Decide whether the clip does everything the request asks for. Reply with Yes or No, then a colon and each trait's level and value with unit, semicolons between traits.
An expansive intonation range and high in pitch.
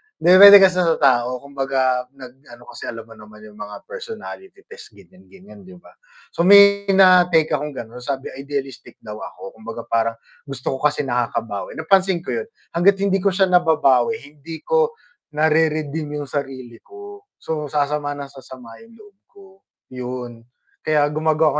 No: wide, 6.7 semitones; medium, 150 Hz